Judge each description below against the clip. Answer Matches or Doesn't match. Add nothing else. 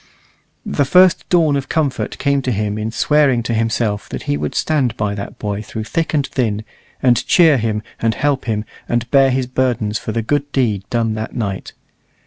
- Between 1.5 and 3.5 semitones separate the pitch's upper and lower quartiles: Doesn't match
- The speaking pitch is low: Matches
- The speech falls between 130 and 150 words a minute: Doesn't match